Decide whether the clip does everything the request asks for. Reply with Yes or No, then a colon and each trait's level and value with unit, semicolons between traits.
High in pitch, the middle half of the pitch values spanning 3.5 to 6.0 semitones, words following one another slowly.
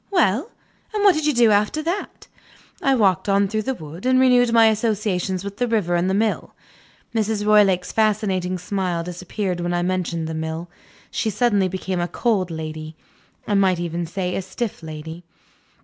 No: high, 195 Hz; average, 4.2 semitones; average, 180 wpm